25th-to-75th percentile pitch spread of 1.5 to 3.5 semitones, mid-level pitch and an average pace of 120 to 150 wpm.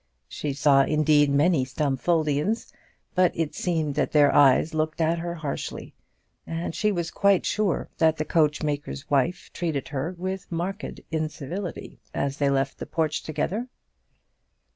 Yes: average, 3.1 semitones; medium, 155 Hz; average, 140 wpm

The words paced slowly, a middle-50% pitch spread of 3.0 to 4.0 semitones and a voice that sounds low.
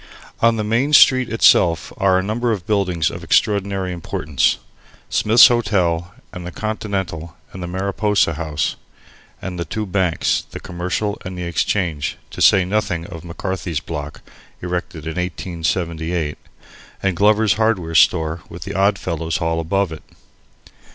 No: average, 145 wpm; average, 3.6 semitones; very low, 90 Hz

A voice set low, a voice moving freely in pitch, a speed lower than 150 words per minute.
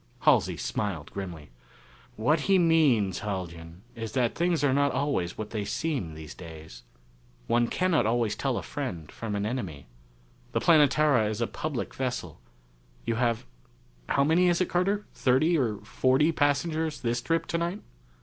No: low, 125 Hz; wide, 7.4 semitones; average, 155 wpm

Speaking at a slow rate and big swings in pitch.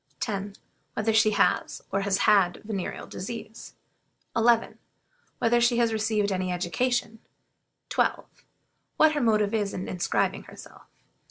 No: slow, 125 wpm; average, 2.7 semitones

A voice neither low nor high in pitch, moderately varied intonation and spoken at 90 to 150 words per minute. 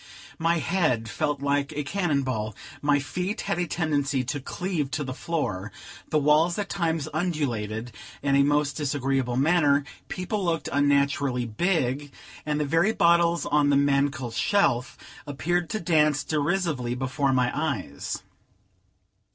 Yes: medium, 145 Hz; average, 3.6 semitones; average, 145 wpm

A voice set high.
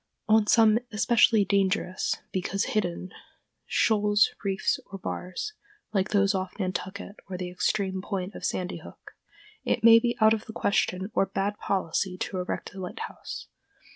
Yes: high, 195 Hz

